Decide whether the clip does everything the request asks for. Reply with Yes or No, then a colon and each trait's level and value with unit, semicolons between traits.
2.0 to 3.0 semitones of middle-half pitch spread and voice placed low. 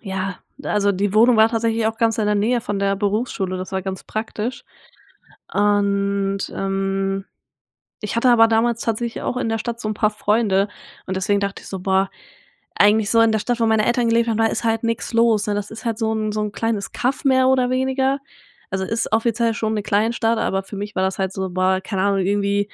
No: narrow, 2.5 semitones; high, 215 Hz